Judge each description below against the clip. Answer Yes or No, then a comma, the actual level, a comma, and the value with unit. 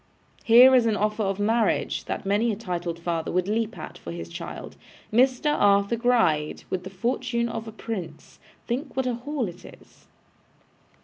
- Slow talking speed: No, average, 175 wpm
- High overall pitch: Yes, high, 220 Hz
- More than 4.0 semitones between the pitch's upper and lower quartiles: Yes, average, 4.5 semitones